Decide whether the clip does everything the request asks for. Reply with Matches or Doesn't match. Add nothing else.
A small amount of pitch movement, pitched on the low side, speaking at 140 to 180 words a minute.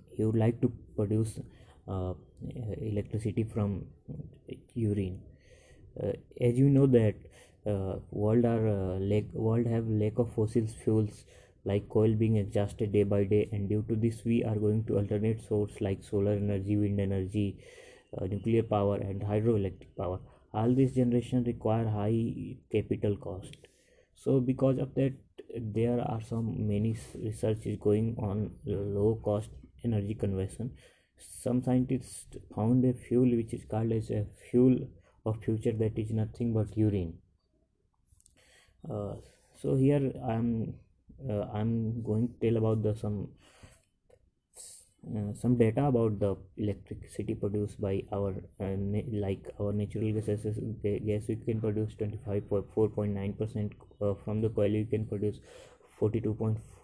Matches